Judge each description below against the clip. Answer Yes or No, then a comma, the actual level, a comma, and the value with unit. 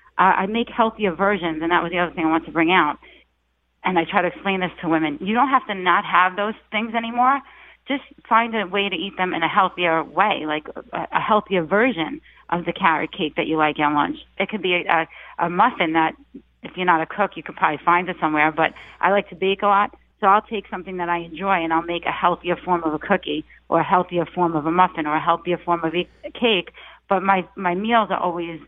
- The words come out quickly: Yes, fast, 250 wpm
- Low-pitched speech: No, medium, 180 Hz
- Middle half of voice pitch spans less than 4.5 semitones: Yes, average, 3.6 semitones